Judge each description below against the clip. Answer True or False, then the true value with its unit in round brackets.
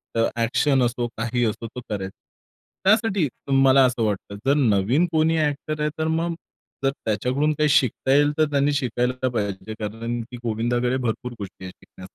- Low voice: True (125 Hz)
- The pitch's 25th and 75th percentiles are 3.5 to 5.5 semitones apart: True (4.5 semitones)